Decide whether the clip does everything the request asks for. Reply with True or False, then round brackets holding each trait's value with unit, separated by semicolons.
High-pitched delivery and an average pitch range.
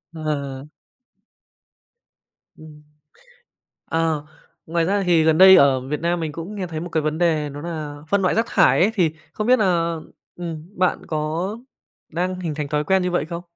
False (165 Hz; 3.0 semitones)